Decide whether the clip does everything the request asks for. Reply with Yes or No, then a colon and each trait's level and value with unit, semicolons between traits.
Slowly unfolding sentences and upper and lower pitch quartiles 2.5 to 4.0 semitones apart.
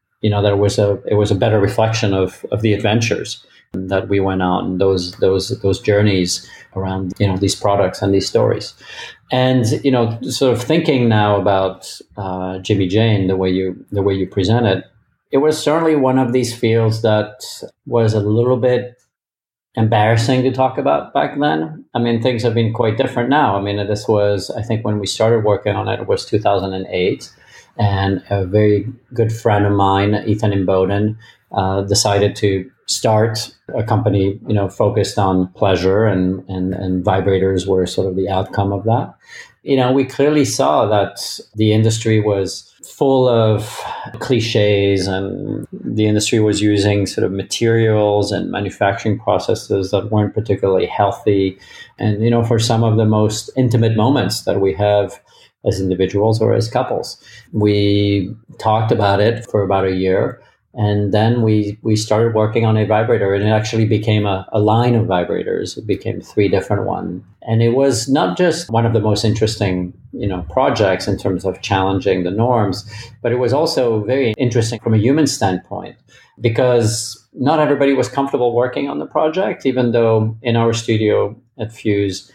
No: average, 175 wpm; average, 2.9 semitones